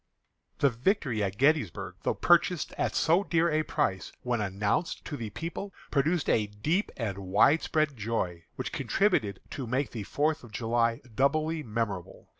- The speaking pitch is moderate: No, low, 125 Hz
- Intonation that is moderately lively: No, wide, 7.0 semitones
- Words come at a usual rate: Yes, average, 155 wpm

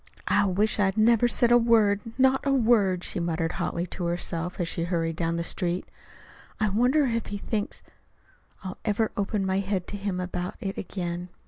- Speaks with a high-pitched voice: Yes, high, 195 Hz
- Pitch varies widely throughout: No, average, 3.8 semitones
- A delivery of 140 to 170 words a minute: No, average, 190 wpm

